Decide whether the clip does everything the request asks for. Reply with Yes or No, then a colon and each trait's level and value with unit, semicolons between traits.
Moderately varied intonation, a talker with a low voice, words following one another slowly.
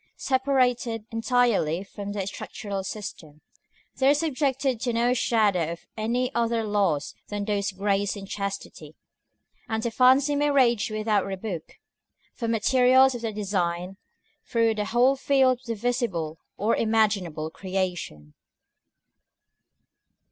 No: average, 4.1 semitones; high, 220 Hz; slow, 130 wpm